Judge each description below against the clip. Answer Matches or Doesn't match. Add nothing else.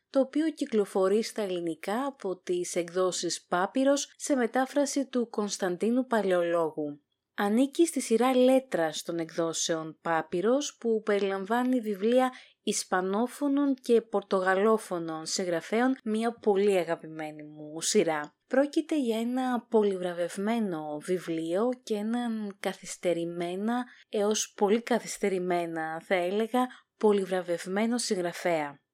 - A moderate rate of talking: Doesn't match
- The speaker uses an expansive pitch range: Matches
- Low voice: Doesn't match